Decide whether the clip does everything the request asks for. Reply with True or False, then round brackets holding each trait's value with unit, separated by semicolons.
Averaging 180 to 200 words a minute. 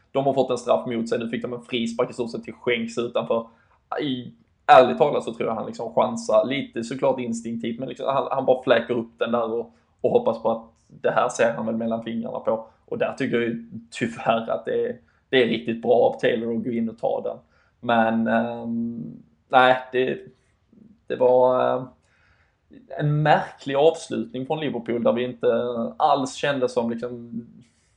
True (195 wpm)